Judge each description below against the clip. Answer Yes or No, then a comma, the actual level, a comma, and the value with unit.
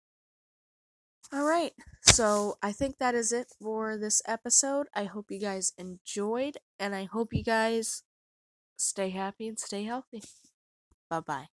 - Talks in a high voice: Yes, high, 220 Hz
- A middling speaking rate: Yes, average, 145 wpm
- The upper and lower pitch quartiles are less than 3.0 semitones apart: No, average, 3.3 semitones